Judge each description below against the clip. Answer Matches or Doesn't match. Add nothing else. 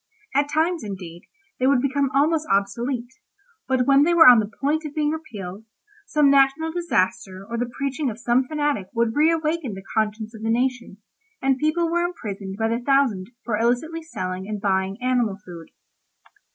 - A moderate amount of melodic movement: Doesn't match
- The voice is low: Doesn't match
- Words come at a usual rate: Matches